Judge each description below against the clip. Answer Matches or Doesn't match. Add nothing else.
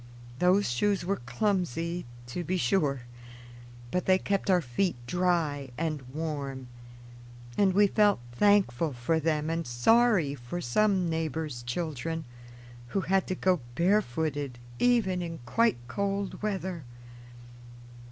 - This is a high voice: Doesn't match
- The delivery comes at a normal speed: Doesn't match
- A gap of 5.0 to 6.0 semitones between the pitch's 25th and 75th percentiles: Matches